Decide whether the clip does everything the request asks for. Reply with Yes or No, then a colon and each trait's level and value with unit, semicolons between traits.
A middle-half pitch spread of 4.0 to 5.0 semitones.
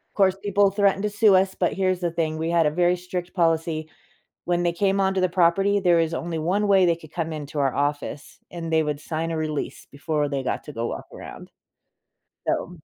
No: average, 3.1 semitones